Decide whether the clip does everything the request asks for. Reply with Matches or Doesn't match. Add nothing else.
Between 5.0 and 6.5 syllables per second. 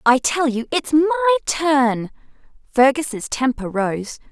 Doesn't match